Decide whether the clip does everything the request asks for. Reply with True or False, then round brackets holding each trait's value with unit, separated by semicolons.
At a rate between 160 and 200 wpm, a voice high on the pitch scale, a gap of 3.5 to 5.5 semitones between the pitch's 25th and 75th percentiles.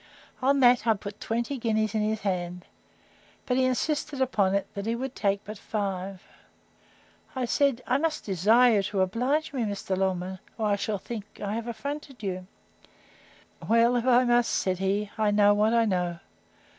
True (180 wpm; 215 Hz; 3.8 semitones)